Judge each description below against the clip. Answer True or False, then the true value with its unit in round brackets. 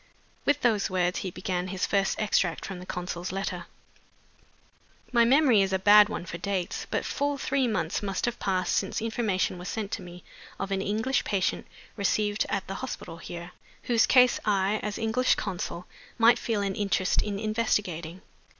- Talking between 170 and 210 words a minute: True (175 wpm)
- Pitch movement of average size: True (3.3 semitones)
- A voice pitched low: False (200 Hz)